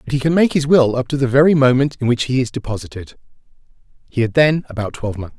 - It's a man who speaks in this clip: Yes, male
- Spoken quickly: Yes, fast, 265 wpm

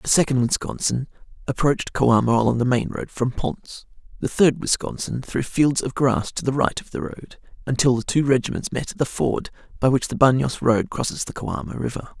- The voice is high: No, low, 130 Hz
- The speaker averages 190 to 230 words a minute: Yes, average, 200 wpm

